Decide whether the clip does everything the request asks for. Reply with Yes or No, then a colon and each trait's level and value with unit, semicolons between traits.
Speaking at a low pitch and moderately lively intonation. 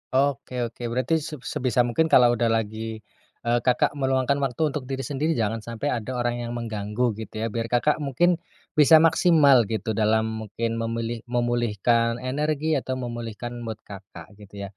Yes: low, 120 Hz; average, 3.0 semitones